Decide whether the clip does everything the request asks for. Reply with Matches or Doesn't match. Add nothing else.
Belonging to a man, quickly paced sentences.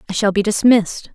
Doesn't match